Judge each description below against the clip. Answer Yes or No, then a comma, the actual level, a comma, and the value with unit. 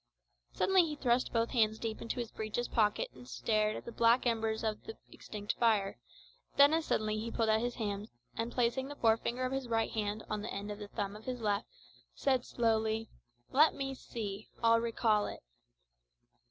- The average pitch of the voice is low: No, high, 225 Hz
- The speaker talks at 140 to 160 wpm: No, average, 195 wpm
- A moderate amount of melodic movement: No, narrow, 2.2 semitones